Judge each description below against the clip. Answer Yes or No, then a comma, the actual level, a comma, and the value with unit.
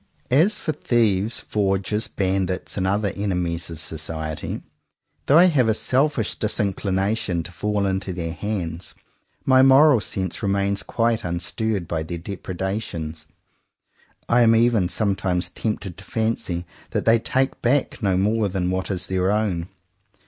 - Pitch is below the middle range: Yes, low, 100 Hz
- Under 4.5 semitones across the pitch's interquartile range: Yes, average, 3.9 semitones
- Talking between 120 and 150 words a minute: Yes, average, 140 wpm